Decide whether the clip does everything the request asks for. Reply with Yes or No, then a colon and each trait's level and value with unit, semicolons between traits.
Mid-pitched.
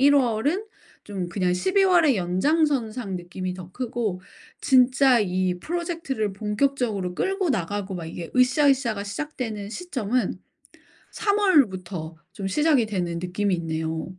No: high, 215 Hz